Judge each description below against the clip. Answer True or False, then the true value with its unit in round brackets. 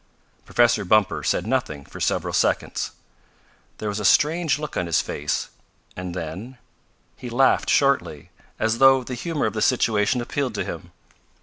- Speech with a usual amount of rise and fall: False (5.8 semitones)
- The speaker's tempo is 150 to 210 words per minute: True (160 wpm)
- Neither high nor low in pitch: False (115 Hz)